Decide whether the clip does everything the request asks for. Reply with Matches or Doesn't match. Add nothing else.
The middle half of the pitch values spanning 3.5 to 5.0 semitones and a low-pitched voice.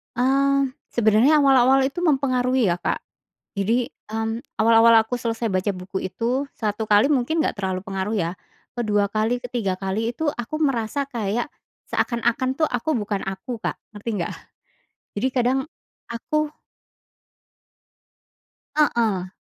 Doesn't match